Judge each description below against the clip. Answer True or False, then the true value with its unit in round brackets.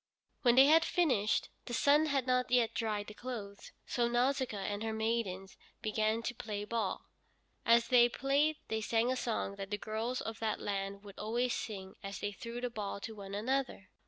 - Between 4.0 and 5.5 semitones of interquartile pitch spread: False (3.3 semitones)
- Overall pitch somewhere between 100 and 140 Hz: False (225 Hz)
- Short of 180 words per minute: False (190 wpm)